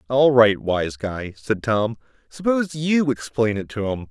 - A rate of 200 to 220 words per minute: No, average, 175 wpm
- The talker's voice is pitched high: No, low, 115 Hz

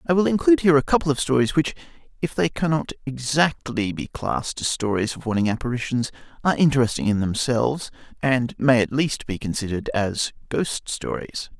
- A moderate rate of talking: Yes, average, 170 wpm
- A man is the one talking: Yes, male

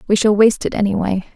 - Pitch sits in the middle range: No, high, 205 Hz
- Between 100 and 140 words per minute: No, fast, 220 wpm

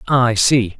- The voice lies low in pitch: Yes, low, 120 Hz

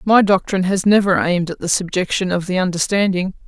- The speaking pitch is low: No, medium, 185 Hz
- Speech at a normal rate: Yes, average, 190 wpm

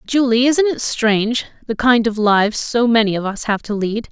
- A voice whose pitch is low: No, high, 230 Hz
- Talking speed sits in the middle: No, fast, 220 wpm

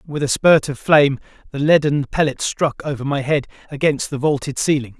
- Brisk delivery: No, average, 190 wpm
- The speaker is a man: Yes, male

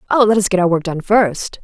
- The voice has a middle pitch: No, high, 195 Hz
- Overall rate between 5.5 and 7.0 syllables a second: Yes, 5.7 syllables/s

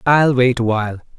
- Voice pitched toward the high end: No, low, 125 Hz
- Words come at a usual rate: Yes, average, 150 wpm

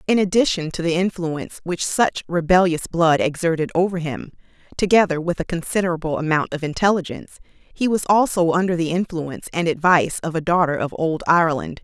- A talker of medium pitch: Yes, medium, 170 Hz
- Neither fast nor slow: Yes, average, 165 wpm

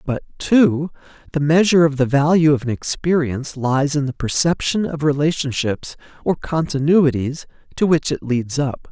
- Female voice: No, male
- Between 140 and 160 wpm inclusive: Yes, average, 155 wpm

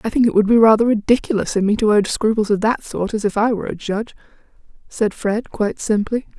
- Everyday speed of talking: No, fast, 235 wpm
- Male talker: No, female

